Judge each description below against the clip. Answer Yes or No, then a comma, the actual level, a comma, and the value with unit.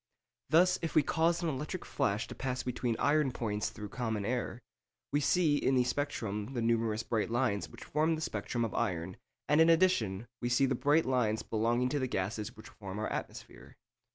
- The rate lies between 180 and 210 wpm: Yes, average, 195 wpm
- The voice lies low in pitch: Yes, low, 125 Hz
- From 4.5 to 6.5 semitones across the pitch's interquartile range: Yes, average, 5.3 semitones